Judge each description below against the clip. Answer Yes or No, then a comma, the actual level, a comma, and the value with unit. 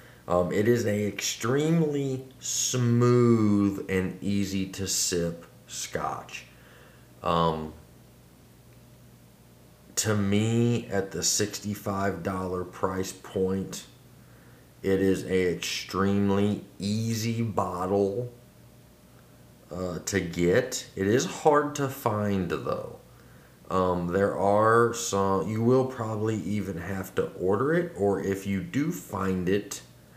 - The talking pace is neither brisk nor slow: No, slow, 105 wpm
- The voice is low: Yes, low, 100 Hz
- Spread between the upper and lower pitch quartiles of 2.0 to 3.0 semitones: No, average, 3.8 semitones